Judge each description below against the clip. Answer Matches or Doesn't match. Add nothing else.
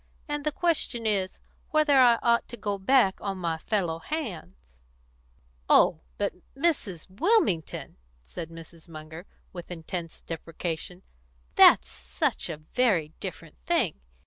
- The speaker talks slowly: Matches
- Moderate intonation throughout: Doesn't match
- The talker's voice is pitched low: Doesn't match